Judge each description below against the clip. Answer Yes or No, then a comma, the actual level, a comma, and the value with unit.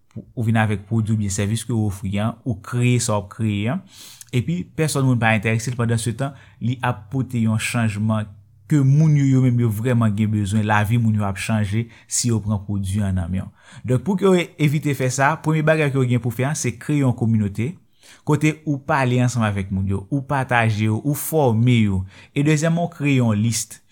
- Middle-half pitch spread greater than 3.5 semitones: Yes, average, 4.0 semitones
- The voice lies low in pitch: Yes, low, 115 Hz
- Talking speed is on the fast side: Yes, fast, 235 wpm